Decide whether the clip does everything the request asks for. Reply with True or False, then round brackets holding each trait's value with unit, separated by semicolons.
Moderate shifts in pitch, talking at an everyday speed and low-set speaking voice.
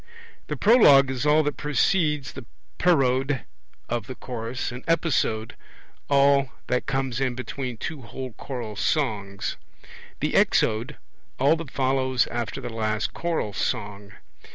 False (3.6 semitones; 130 wpm; 130 Hz)